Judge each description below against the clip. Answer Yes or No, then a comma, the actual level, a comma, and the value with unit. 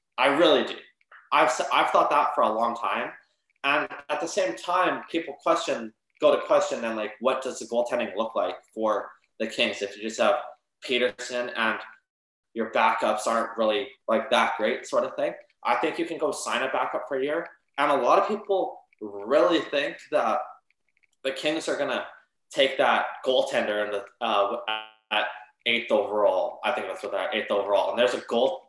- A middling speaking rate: Yes, average, 190 wpm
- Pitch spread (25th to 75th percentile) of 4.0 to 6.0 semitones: No, average, 2.7 semitones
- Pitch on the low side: Yes, low, 115 Hz